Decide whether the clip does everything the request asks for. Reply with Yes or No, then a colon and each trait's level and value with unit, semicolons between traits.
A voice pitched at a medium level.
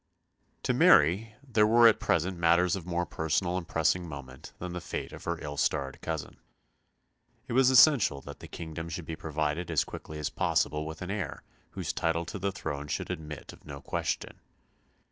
No: very low, 85 Hz